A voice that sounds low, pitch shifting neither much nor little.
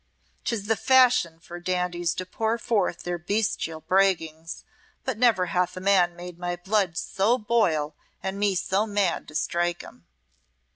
No: medium, 185 Hz; average, 3.2 semitones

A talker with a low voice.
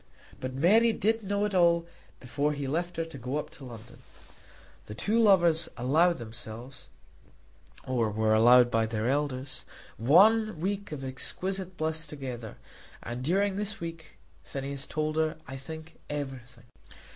No: medium, 150 Hz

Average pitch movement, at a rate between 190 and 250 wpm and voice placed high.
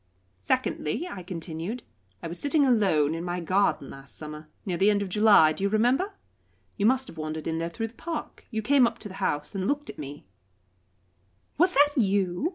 No: wide, 7.3 semitones; fast, 205 wpm; high, 195 Hz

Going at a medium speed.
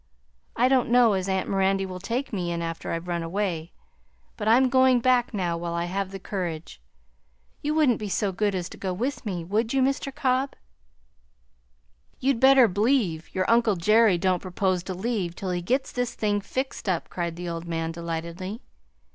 Yes: average, 190 wpm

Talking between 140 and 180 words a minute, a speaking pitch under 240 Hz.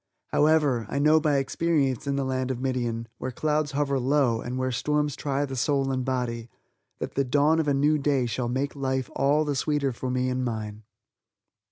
No: average, 200 wpm; low, 135 Hz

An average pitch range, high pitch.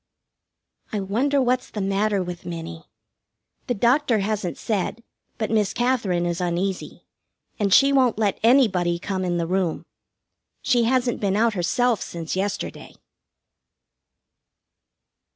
Yes: average, 5.0 semitones; high, 205 Hz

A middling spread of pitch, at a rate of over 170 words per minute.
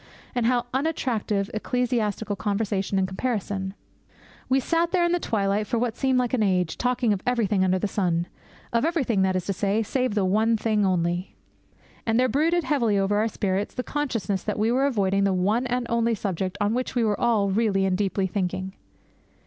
Yes: average, 4.1 semitones; average, 190 wpm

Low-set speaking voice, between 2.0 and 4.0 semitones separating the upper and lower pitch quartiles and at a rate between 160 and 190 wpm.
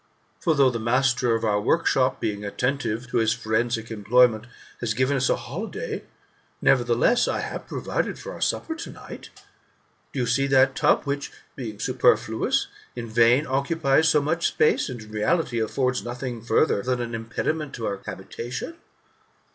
Yes: low, 125 Hz; average, 3.3 semitones; average, 165 wpm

